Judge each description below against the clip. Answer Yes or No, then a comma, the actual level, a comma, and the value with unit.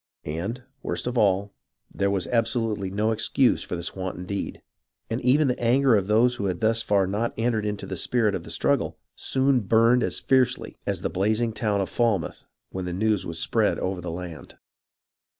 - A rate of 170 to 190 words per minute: Yes, average, 185 wpm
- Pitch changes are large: No, average, 3.8 semitones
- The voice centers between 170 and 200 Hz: No, low, 110 Hz